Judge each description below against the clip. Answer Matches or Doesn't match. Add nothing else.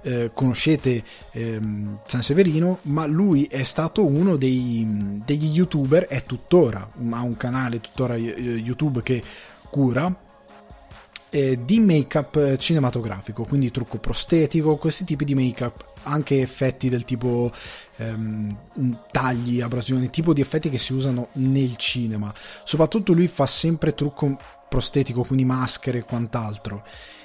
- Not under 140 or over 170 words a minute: Doesn't match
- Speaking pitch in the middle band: Doesn't match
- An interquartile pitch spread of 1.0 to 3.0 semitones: Doesn't match